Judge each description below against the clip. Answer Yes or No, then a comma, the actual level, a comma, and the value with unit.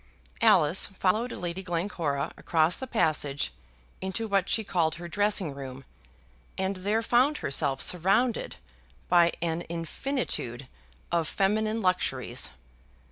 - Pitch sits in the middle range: Yes, medium, 180 Hz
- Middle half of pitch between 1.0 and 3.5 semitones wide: No, average, 4.7 semitones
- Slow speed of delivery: Yes, slow, 115 wpm